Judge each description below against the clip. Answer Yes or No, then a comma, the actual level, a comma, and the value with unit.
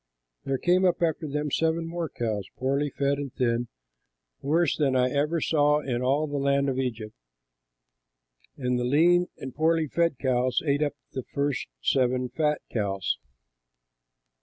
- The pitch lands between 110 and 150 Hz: Yes, medium, 140 Hz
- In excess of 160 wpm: No, average, 155 wpm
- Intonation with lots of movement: No, average, 3.5 semitones